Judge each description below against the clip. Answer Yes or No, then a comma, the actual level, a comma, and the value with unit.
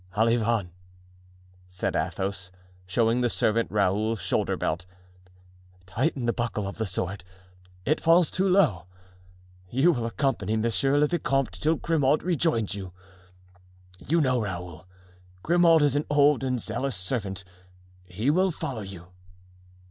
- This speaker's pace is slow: Yes, slow, 130 wpm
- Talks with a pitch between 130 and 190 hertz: No, low, 115 Hz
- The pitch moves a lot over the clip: Yes, wide, 6.9 semitones